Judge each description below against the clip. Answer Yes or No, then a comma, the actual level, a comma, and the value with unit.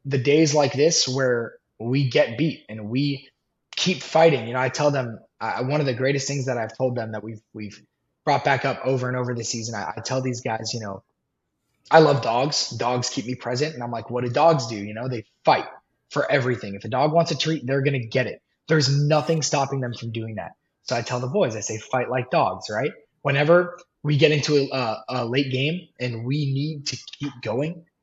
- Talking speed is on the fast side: Yes, fast, 230 wpm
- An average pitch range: Yes, average, 3.5 semitones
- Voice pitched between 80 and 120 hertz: No, low, 130 Hz